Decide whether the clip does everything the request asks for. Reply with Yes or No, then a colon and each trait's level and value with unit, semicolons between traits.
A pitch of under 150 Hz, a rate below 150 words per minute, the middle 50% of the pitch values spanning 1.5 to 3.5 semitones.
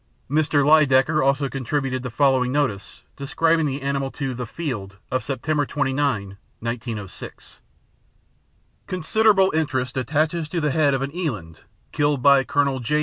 Yes: medium, 140 Hz; average, 140 wpm; average, 2.9 semitones